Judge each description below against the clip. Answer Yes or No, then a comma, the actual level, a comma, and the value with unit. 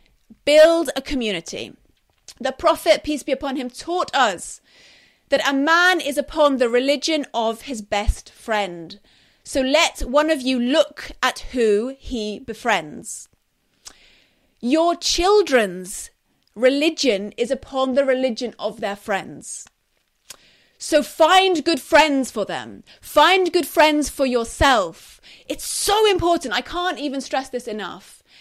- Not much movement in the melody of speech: No, average, 4.9 semitones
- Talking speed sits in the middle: No, slow, 130 wpm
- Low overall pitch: No, very high, 275 Hz